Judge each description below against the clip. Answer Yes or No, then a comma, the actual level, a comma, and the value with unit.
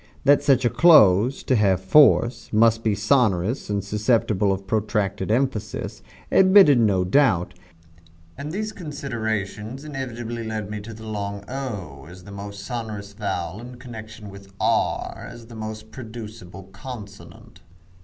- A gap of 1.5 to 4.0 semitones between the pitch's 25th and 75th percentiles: Yes, average, 3.7 semitones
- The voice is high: No, low, 110 Hz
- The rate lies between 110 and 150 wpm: Yes, average, 140 wpm